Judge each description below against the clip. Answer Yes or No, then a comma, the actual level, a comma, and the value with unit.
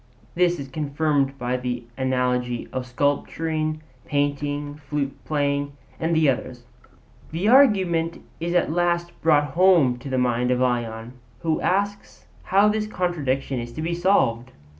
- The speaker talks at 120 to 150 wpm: Yes, average, 145 wpm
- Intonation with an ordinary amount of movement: Yes, average, 5.0 semitones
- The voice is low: No, medium, 145 Hz